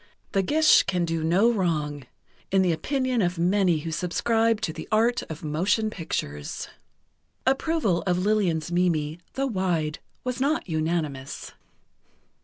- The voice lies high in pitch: No, medium, 180 Hz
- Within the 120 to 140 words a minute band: Yes, slow, 135 wpm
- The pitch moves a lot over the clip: Yes, wide, 5.7 semitones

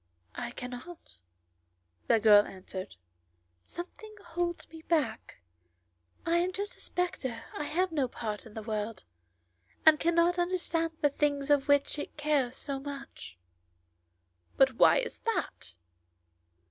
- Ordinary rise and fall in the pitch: No, wide, 6.2 semitones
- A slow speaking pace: Yes, slow, 130 wpm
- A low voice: No, very high, 290 Hz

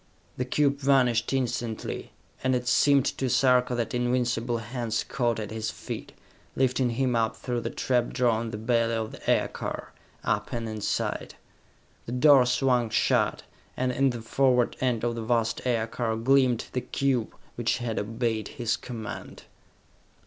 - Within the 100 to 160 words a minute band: Yes, average, 155 wpm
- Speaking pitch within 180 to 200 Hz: No, low, 120 Hz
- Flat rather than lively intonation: Yes, narrow, 1.9 semitones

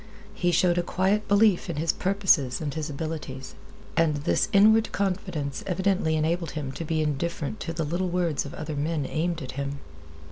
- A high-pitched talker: No, medium, 165 Hz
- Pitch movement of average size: Yes, average, 3.6 semitones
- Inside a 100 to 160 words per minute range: No, average, 175 wpm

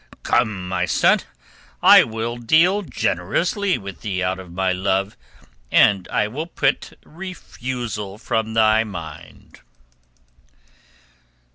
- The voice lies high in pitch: No, low, 110 Hz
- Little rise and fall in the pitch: No, average, 4.6 semitones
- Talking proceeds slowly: Yes, slow, 115 wpm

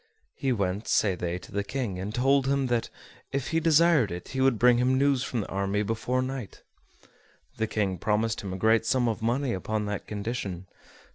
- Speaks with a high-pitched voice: No, low, 115 Hz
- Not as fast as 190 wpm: No, average, 200 wpm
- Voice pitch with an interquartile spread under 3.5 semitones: No, average, 4.5 semitones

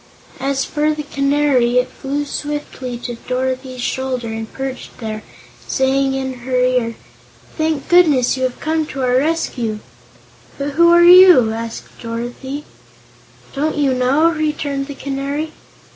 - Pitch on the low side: No, very high, 270 Hz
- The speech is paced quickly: No, average, 140 wpm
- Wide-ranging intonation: No, average, 2.8 semitones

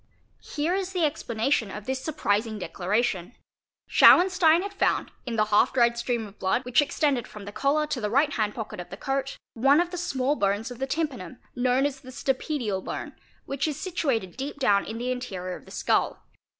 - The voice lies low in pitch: No, very high, 255 Hz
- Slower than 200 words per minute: No, fast, 205 wpm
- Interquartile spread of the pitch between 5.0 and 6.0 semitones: Yes, wide, 5.5 semitones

